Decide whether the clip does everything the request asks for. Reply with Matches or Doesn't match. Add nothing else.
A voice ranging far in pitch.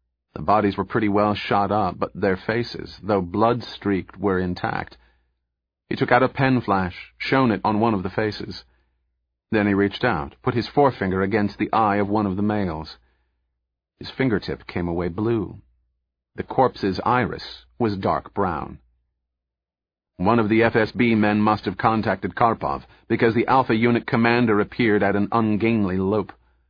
Matches